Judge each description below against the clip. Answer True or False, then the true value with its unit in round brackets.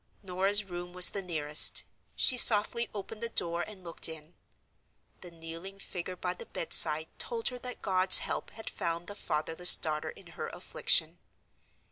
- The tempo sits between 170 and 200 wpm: False (160 wpm)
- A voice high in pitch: False (180 Hz)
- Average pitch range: True (3.5 semitones)